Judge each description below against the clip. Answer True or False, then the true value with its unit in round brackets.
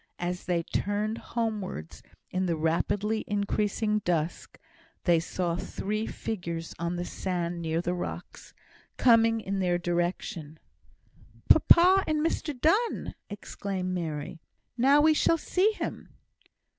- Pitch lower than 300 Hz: True (190 Hz)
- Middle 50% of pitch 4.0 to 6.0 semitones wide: True (4.7 semitones)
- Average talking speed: False (120 wpm)